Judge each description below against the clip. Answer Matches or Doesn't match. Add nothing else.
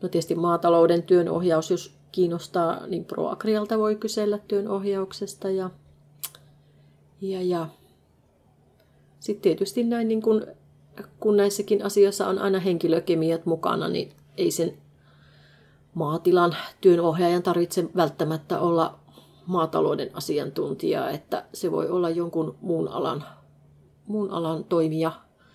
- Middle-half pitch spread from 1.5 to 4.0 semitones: Matches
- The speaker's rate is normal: Matches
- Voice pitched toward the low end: Doesn't match